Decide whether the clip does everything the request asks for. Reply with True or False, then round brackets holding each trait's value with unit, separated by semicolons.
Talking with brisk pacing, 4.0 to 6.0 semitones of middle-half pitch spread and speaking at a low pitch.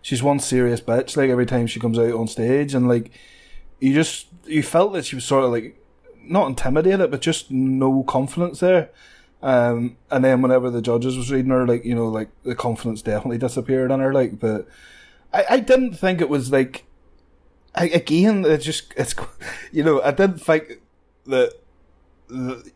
False (185 wpm; 4.7 semitones; 130 Hz)